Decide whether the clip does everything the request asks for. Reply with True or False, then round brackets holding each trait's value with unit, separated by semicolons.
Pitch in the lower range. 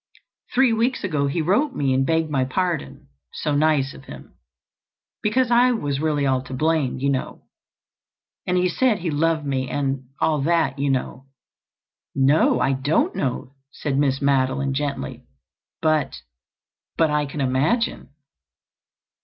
False (145 Hz)